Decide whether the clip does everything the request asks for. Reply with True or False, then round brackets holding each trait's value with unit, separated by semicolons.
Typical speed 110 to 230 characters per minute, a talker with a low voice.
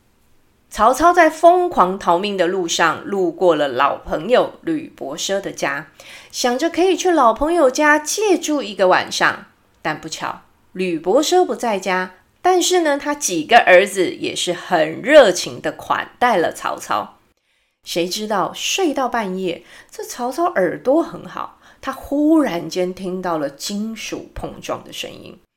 False (215 characters per minute; 245 Hz)